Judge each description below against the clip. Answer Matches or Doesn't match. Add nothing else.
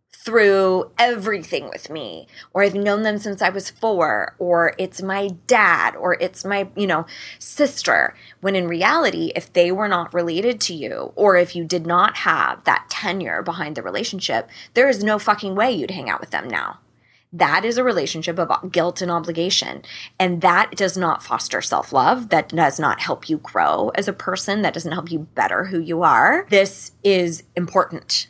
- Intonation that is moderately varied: Matches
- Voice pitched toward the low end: Doesn't match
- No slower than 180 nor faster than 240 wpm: Matches